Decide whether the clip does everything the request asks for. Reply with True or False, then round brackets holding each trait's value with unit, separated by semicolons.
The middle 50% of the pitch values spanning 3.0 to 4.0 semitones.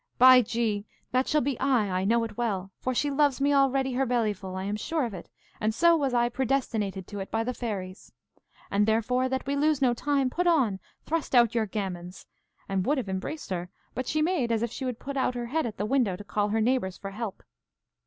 False (4.7 semitones)